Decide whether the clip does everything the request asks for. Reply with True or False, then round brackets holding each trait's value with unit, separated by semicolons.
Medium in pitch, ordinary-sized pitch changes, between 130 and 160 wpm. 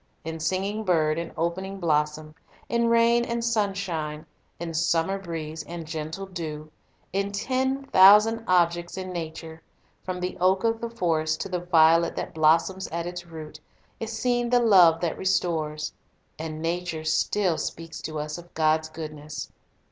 True (170 Hz; 3.6 semitones; 155 wpm)